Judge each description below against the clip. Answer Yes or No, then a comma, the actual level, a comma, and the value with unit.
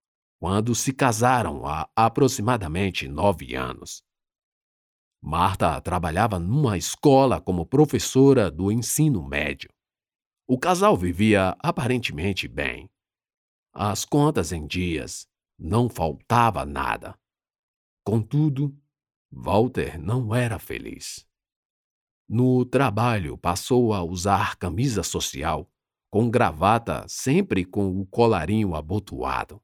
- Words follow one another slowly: Yes, slow, 95 wpm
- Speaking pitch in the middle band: No, low, 105 Hz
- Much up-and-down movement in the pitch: Yes, wide, 5.8 semitones